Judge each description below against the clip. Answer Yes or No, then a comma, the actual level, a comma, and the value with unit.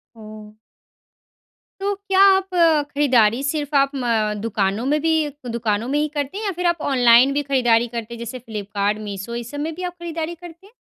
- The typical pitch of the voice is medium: No, very high, 270 Hz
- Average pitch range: No, wide, 6.0 semitones